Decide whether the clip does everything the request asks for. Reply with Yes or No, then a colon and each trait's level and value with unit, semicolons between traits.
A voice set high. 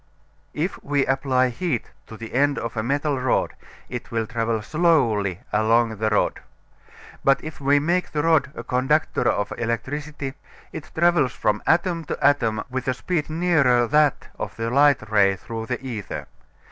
No: low, 130 Hz